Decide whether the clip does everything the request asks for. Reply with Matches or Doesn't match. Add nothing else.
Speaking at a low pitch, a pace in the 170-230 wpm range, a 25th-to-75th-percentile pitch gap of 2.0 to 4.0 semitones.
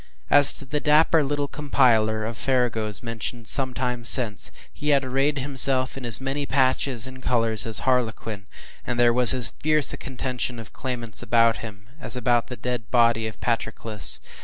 Matches